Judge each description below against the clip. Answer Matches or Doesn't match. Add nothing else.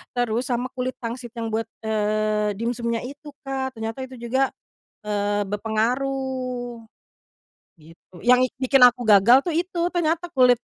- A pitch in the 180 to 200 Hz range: Doesn't match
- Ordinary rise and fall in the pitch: Matches